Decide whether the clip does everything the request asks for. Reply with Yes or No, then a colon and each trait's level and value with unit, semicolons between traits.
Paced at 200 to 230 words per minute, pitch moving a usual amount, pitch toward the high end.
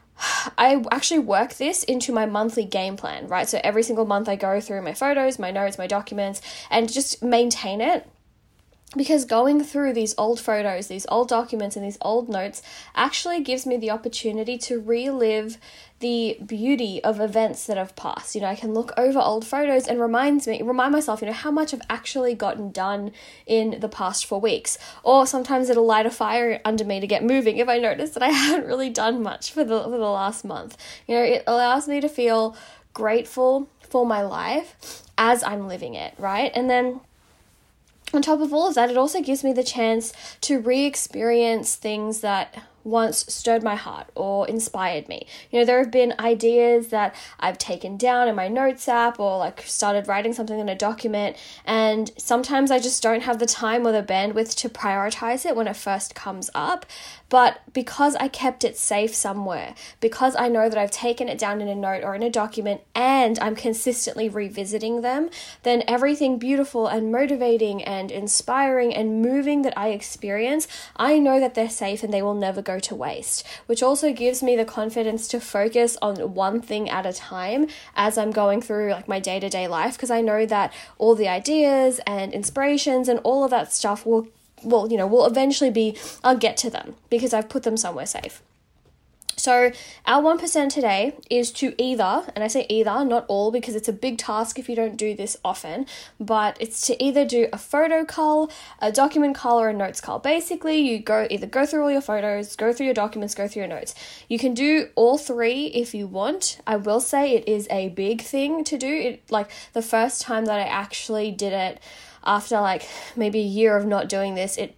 Yes: fast, 205 wpm; average, 3.4 semitones; high, 230 Hz